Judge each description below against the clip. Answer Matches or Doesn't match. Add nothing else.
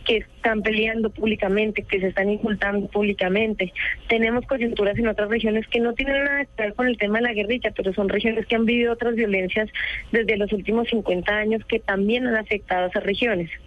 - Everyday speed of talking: Doesn't match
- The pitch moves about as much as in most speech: Doesn't match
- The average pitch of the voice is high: Matches